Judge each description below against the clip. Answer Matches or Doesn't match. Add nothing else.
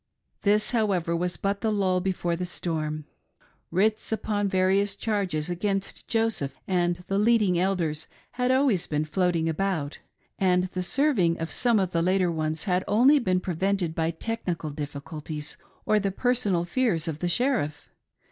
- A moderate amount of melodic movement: Matches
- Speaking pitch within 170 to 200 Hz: Matches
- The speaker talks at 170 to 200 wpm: Doesn't match